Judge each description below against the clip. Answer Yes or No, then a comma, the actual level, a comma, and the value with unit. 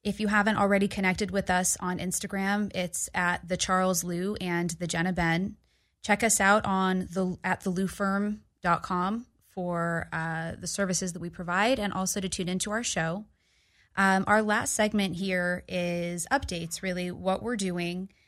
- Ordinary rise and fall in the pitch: No, narrow, 2.2 semitones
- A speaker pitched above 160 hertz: Yes, medium, 185 Hz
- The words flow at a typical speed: Yes, average, 165 wpm